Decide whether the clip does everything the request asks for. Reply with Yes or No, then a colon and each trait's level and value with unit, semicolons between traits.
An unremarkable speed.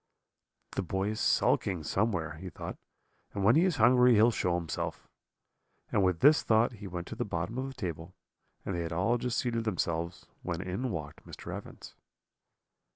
Yes: average, 185 wpm